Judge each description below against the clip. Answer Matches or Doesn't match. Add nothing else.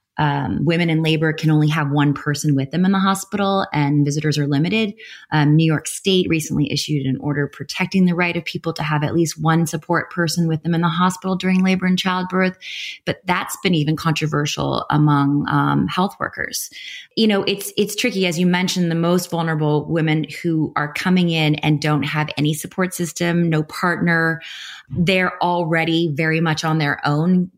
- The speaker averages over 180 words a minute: Matches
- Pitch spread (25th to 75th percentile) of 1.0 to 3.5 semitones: Matches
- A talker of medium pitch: Matches